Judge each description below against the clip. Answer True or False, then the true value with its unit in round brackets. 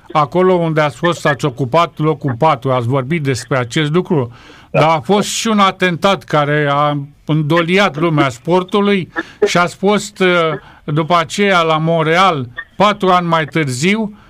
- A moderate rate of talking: True (145 wpm)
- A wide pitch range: False (3.5 semitones)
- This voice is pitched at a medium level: True (165 Hz)